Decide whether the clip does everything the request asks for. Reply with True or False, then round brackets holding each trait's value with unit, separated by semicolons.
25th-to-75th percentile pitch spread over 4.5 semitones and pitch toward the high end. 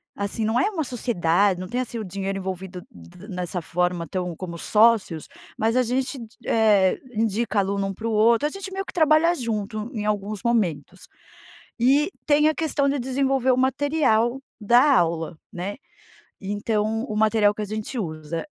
True (5.0 semitones; 215 Hz)